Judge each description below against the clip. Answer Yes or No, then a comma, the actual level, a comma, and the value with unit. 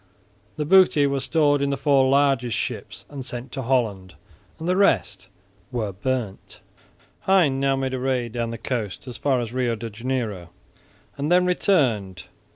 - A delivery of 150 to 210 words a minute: Yes, average, 165 wpm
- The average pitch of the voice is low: Yes, low, 130 Hz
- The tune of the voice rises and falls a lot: No, average, 3.5 semitones